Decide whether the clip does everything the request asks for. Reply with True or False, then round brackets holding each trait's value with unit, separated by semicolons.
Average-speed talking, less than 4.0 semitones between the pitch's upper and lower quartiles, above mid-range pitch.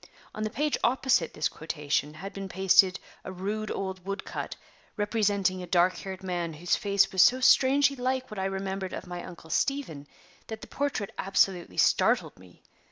True (175 wpm; 3.3 semitones; 195 Hz)